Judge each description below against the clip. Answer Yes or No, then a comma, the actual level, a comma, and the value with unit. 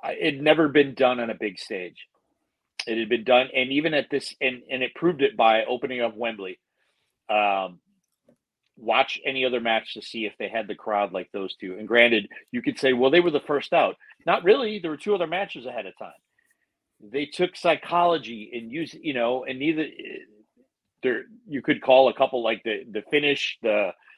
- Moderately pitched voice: No, low, 130 Hz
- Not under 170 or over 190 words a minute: No, fast, 205 wpm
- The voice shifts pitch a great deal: Yes, wide, 5.9 semitones